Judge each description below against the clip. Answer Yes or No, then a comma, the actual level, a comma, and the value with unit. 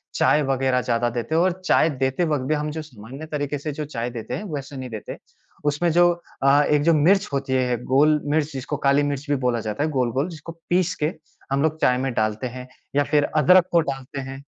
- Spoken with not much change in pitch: No, average, 3.0 semitones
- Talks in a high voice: No, medium, 140 Hz